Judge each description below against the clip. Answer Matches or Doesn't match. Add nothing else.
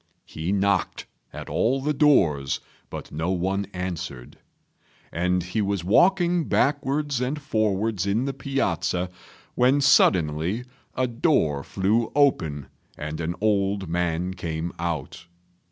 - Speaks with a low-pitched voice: Matches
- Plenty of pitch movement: Matches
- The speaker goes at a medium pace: Doesn't match